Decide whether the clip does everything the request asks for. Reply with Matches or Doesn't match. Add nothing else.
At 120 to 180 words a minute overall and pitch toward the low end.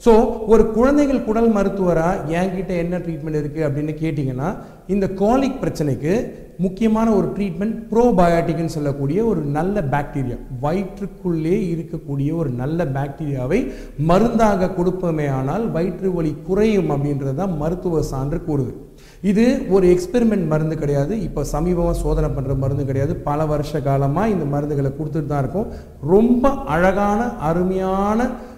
Doesn't match